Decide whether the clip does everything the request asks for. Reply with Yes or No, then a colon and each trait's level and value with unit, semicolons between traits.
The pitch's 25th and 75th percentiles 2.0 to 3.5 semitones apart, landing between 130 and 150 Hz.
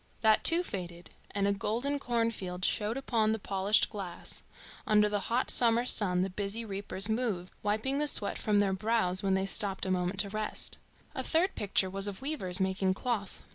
No: average, 3.2 semitones; high, 205 Hz